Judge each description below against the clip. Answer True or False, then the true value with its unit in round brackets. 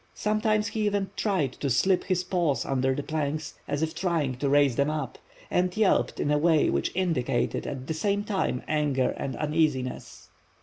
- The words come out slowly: False (180 wpm)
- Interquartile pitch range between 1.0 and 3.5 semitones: False (5.3 semitones)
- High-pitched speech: False (155 Hz)